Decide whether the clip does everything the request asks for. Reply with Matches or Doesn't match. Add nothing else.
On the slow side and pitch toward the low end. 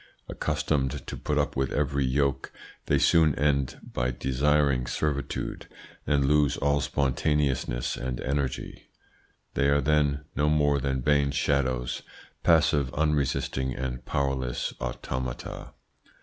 Matches